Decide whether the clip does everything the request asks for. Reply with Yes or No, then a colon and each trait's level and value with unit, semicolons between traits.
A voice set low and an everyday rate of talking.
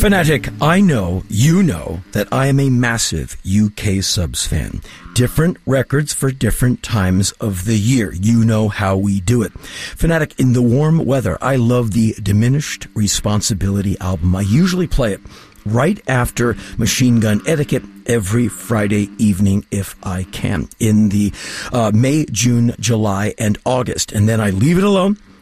Yes: low, 115 Hz; average, 160 wpm